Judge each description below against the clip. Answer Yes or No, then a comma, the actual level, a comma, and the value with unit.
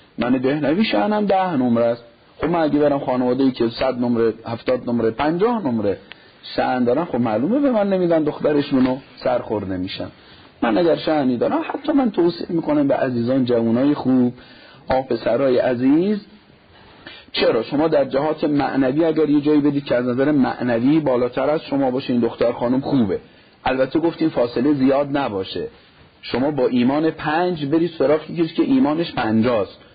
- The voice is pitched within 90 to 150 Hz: Yes, medium, 140 Hz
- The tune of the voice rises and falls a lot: No, average, 4.9 semitones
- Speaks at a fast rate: Yes, fast, 160 wpm